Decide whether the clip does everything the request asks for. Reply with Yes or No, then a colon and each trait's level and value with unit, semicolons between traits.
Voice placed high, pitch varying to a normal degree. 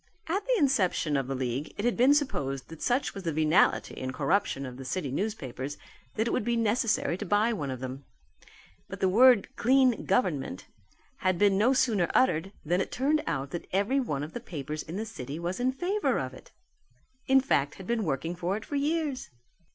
No: high, 195 Hz; wide, 8.8 semitones